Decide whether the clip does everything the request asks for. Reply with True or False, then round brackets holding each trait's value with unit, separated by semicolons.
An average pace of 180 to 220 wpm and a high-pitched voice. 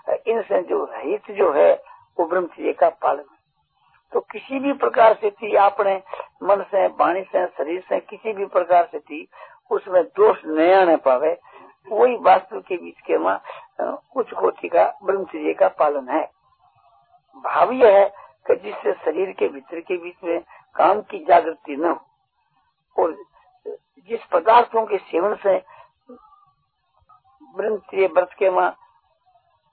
False (140 wpm; 235 Hz)